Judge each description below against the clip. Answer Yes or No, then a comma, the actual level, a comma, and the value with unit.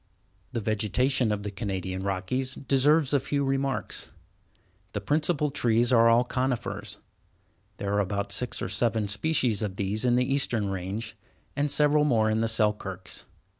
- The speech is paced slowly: No, average, 155 wpm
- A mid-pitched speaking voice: No, low, 115 Hz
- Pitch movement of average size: Yes, average, 4.7 semitones